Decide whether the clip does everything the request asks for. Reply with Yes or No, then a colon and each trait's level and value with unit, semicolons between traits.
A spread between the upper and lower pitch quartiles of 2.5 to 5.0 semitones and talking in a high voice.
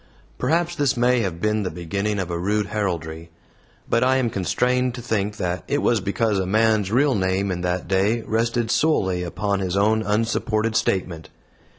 No: average, 3.8 semitones; low, 105 Hz